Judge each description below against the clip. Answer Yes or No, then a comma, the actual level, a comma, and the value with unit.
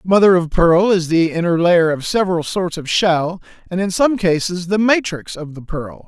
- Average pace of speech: No, fast, 210 wpm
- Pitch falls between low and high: Yes, medium, 175 Hz